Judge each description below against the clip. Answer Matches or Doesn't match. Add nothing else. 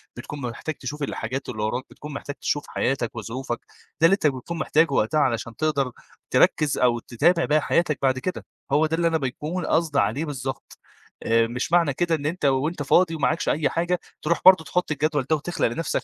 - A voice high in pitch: Doesn't match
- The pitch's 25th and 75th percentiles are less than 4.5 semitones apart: Matches